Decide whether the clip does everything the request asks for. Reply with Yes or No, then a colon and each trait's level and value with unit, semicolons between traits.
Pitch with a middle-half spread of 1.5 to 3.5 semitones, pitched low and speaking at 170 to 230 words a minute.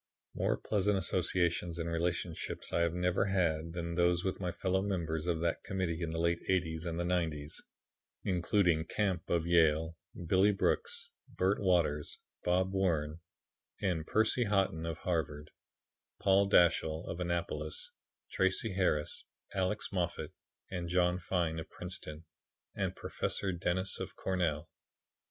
No: narrow, 2.4 semitones; very low, 85 Hz; average, 140 wpm